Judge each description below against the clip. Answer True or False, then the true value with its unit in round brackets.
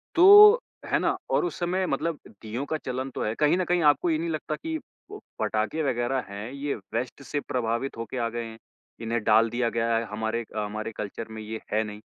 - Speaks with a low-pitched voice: True (120 Hz)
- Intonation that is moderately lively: False (5.8 semitones)